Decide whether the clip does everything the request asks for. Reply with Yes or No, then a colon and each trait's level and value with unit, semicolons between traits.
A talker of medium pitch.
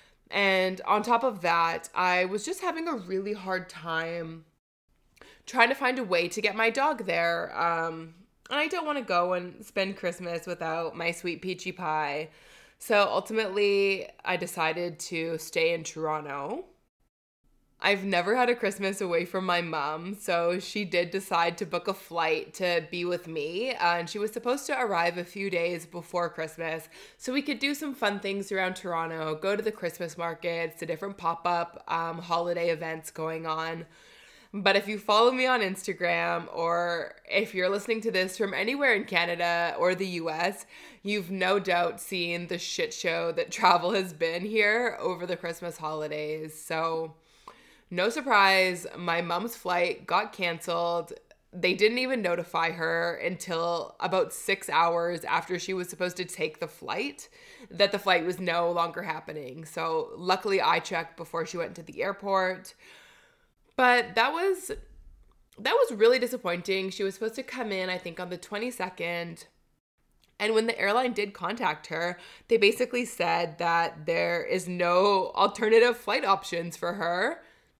Yes: medium, 180 Hz